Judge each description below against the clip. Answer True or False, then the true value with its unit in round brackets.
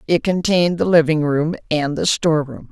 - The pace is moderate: True (175 wpm)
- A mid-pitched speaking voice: True (155 Hz)